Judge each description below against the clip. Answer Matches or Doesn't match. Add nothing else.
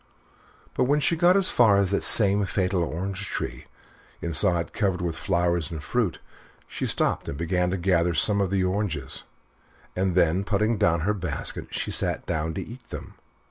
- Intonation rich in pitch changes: Doesn't match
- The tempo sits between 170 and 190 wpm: Matches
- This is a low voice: Matches